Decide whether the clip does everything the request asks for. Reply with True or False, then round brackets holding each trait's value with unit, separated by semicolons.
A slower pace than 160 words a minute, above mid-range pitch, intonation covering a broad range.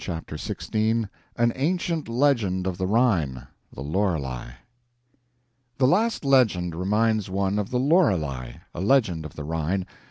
False (135 wpm; 100 Hz; 7.2 semitones)